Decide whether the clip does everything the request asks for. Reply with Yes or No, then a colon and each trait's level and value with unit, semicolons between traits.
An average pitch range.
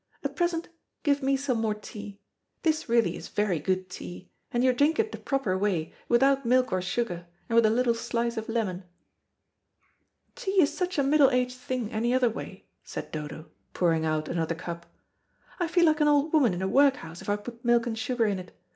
No: wide, 6.4 semitones